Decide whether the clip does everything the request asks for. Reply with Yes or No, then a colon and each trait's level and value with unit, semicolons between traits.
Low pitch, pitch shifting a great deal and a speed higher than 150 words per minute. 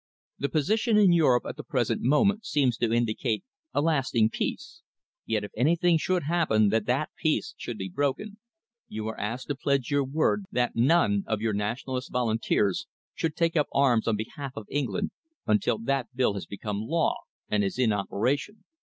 Yes: low, 125 Hz; wide, 5.8 semitones; average, 175 wpm